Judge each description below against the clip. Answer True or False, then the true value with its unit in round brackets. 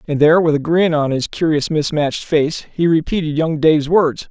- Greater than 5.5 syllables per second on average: False (5.4 syllables/s)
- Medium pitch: True (155 Hz)